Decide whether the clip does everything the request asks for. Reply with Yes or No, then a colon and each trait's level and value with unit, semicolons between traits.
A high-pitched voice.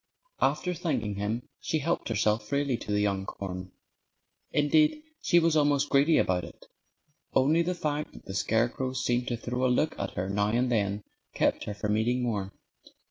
No: low, 120 Hz